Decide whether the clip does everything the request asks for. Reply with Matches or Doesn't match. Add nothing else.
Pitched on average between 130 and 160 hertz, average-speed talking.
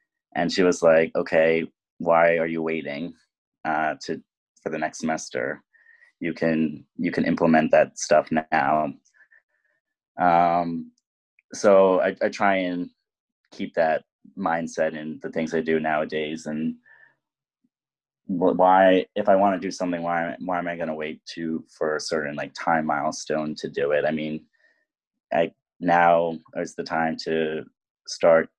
Doesn't match